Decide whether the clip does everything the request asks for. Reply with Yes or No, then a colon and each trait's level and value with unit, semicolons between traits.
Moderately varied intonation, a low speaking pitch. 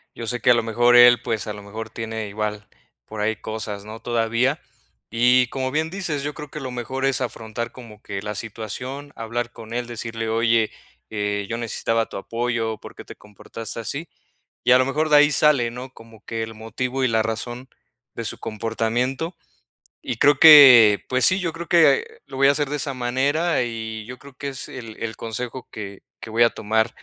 Yes: average, 3.0 semitones; low, 120 Hz